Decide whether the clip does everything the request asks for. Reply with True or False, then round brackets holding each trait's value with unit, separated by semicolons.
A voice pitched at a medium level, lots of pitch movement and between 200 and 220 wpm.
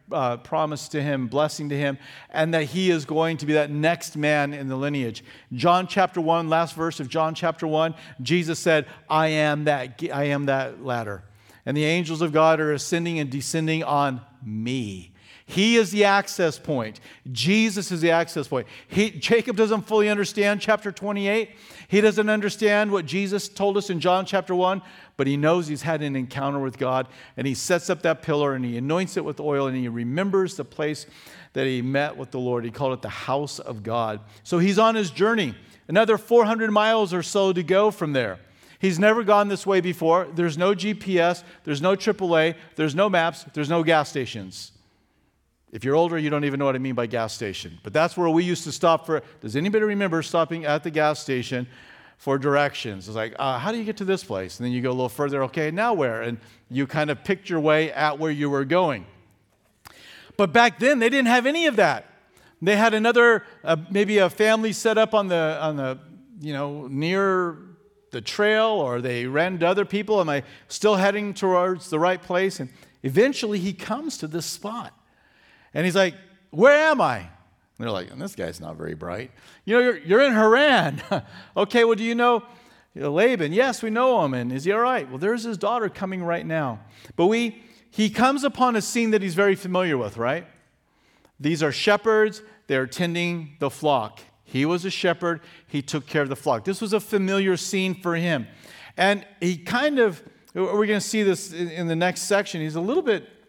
True (165 Hz; 6.3 semitones; 205 wpm)